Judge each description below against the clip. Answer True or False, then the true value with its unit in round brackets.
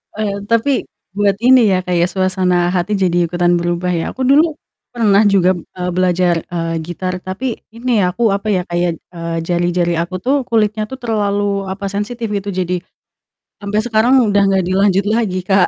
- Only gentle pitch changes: False (3.1 semitones)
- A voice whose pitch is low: False (190 Hz)